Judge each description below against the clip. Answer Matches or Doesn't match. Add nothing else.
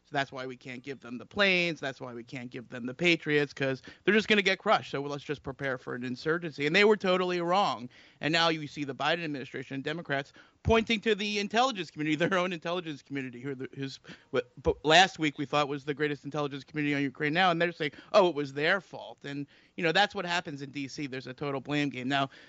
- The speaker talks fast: Matches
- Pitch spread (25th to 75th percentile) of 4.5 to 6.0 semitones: Doesn't match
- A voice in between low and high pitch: Matches